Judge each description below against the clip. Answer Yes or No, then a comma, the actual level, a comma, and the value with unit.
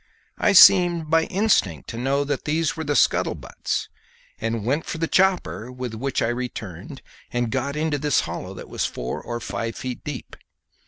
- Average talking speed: Yes, average, 175 wpm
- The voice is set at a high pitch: No, low, 135 Hz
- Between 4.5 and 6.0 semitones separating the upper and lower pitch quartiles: Yes, average, 5.2 semitones